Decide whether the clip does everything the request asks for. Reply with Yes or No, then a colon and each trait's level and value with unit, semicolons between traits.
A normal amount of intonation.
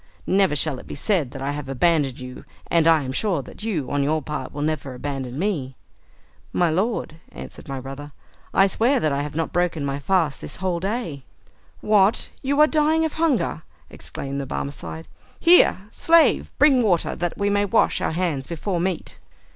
No: wide, 6.4 semitones